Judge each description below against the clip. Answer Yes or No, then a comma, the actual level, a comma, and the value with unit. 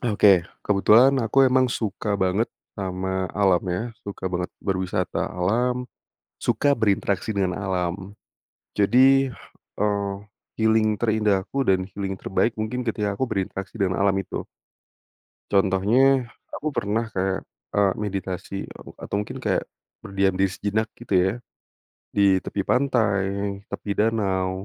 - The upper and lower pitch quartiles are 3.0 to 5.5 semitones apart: No, narrow, 2.5 semitones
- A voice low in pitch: Yes, low, 100 Hz